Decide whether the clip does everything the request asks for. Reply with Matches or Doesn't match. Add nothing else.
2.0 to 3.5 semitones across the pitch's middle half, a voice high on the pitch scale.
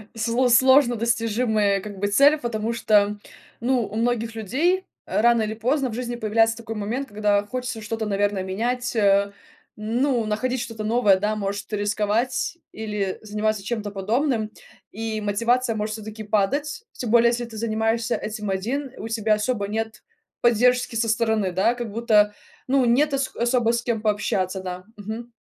Matches